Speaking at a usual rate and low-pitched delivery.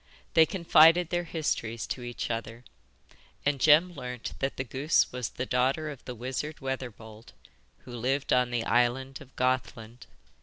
Yes: average, 155 wpm; low, 130 Hz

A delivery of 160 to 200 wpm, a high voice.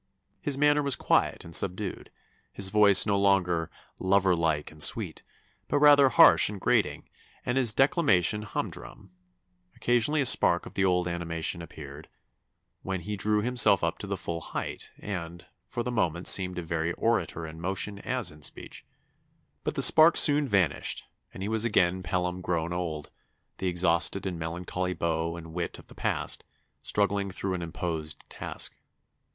No: average, 165 wpm; very low, 95 Hz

